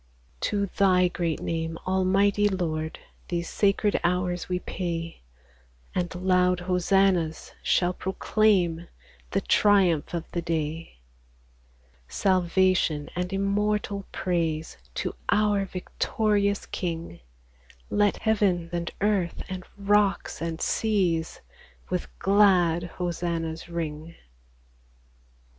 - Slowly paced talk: Yes, slow, 100 wpm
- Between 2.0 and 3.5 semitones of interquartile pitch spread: Yes, average, 2.8 semitones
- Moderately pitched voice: Yes, medium, 180 Hz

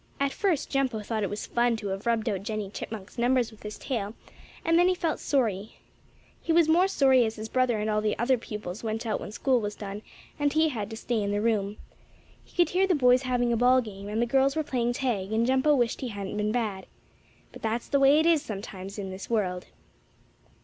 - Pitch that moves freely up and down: No, average, 4.1 semitones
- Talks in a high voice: Yes, high, 230 Hz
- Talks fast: Yes, fast, 235 wpm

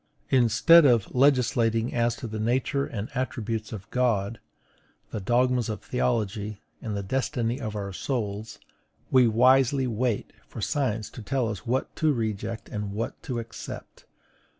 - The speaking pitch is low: Yes, low, 115 Hz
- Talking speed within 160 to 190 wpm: No, average, 150 wpm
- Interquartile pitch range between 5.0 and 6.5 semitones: No, average, 2.9 semitones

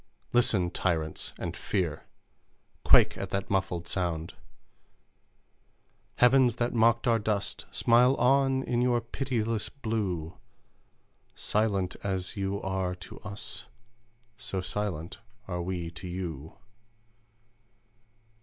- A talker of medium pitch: No, low, 100 Hz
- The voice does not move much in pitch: No, average, 4.7 semitones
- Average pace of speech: No, slow, 105 wpm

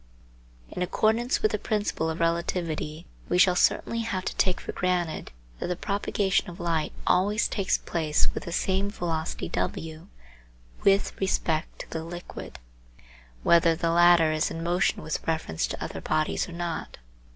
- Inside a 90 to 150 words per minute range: No, average, 160 wpm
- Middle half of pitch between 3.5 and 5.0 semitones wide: No, average, 2.7 semitones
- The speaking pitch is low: No, medium, 175 Hz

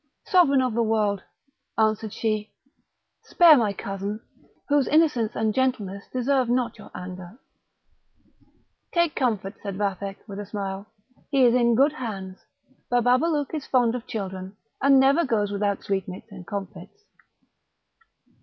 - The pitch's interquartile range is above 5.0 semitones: No, average, 4.6 semitones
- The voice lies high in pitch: Yes, high, 220 Hz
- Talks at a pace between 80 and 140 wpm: Yes, slow, 135 wpm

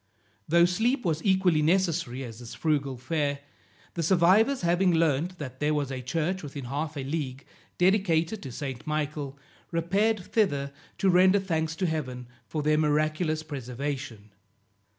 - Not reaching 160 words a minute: Yes, average, 150 wpm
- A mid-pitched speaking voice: Yes, medium, 155 Hz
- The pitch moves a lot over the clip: No, average, 4.3 semitones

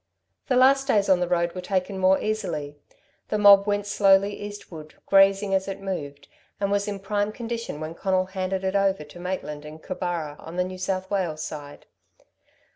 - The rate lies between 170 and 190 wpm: Yes, average, 185 wpm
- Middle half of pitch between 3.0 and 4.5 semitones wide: No, narrow, 2.6 semitones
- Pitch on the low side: No, high, 190 Hz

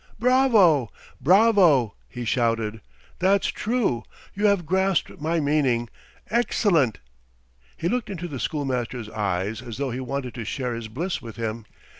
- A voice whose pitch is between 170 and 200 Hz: No, medium, 140 Hz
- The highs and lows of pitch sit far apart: Yes, wide, 8.4 semitones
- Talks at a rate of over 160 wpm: No, average, 145 wpm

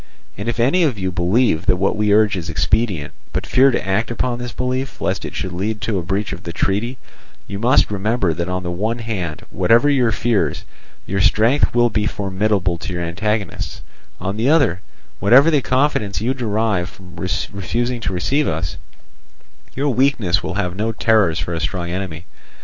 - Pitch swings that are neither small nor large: Yes, average, 4.6 semitones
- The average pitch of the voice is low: Yes, low, 105 Hz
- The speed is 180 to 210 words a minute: Yes, average, 190 wpm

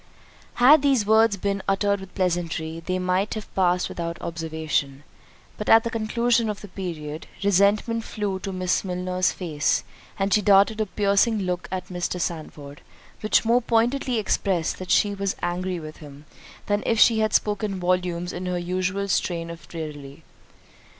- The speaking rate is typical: Yes, average, 165 wpm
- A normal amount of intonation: Yes, average, 3.3 semitones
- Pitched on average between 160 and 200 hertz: Yes, medium, 185 Hz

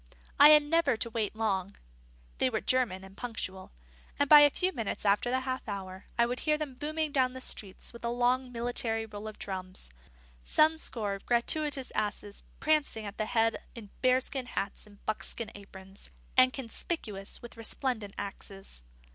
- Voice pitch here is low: No, high, 235 Hz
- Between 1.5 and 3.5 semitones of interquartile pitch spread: No, average, 4.3 semitones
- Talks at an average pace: Yes, average, 170 wpm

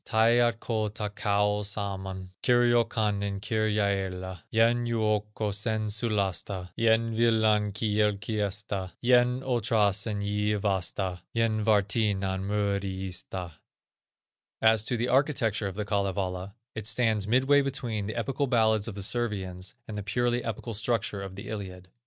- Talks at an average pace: No, slow, 115 wpm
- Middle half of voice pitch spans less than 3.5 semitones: Yes, narrow, 2.5 semitones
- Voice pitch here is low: Yes, low, 105 Hz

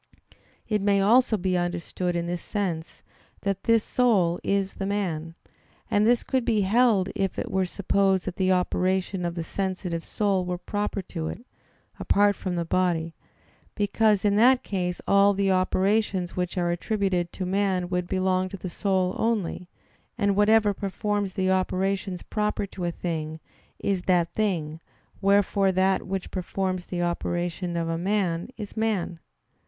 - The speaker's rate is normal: Yes, average, 160 wpm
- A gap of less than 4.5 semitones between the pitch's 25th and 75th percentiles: Yes, narrow, 2.4 semitones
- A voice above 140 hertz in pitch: Yes, high, 190 Hz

